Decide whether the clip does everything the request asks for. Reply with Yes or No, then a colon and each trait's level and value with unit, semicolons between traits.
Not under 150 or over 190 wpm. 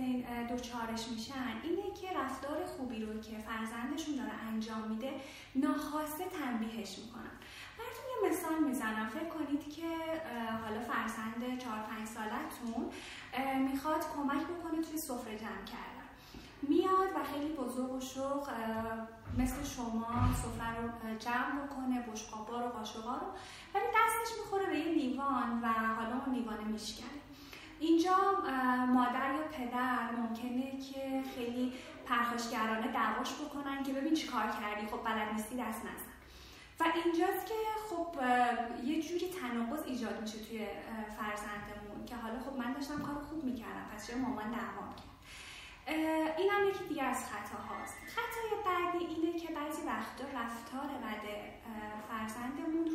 No: average, 135 wpm